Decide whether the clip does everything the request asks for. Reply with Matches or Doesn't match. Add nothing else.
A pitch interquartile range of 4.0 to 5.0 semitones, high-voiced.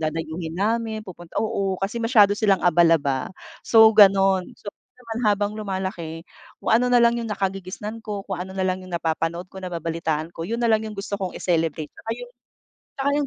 Matches